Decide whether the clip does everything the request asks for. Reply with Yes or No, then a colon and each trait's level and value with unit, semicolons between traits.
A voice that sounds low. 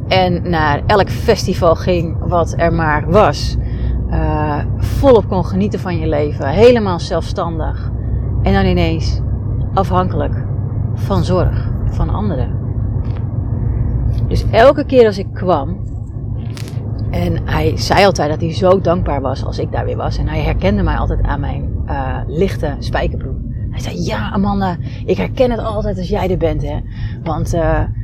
Yes: low, 110 Hz